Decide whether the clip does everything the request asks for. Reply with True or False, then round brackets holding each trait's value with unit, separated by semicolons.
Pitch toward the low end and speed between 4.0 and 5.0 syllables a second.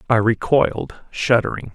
True (115 Hz; 4.6 syllables/s)